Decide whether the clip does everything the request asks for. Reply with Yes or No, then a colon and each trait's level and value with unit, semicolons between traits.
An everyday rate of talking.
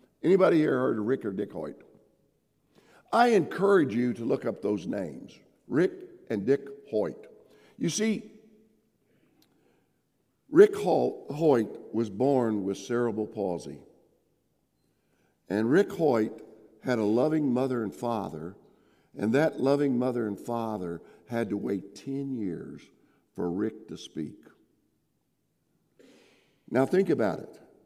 No: slow, 125 wpm